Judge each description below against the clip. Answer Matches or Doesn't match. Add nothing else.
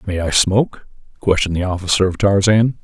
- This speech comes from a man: Matches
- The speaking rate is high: Doesn't match